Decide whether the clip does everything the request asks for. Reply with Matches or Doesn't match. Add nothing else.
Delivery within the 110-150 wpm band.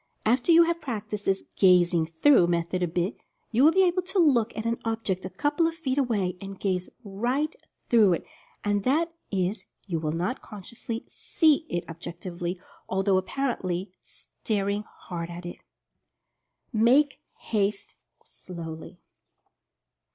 Matches